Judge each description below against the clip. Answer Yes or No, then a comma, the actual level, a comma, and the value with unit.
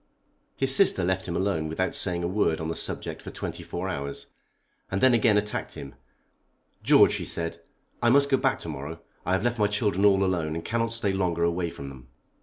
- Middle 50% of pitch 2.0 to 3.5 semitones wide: No, average, 4.1 semitones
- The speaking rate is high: Yes, fast, 210 wpm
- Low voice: Yes, very low, 95 Hz